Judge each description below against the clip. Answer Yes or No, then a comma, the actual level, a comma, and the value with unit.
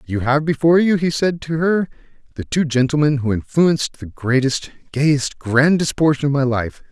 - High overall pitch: No, medium, 145 Hz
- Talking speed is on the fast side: No, average, 180 wpm